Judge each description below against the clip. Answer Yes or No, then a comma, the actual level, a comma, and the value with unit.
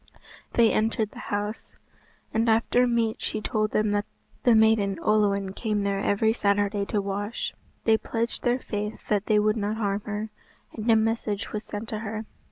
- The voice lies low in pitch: No, high, 215 Hz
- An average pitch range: No, narrow, 1.5 semitones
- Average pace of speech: Yes, average, 175 wpm